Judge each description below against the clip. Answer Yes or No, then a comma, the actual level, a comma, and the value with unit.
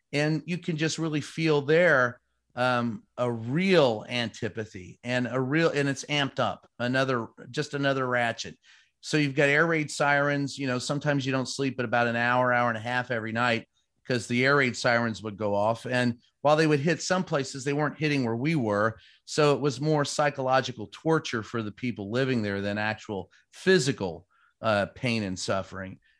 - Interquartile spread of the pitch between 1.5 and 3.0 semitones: No, average, 3.8 semitones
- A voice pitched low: Yes, low, 130 Hz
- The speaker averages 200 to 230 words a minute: No, average, 190 wpm